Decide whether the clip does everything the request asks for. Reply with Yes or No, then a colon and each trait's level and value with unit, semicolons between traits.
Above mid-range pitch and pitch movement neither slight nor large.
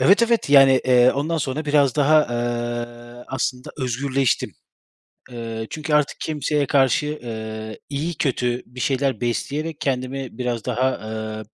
No: low, 130 Hz; average, 3.3 semitones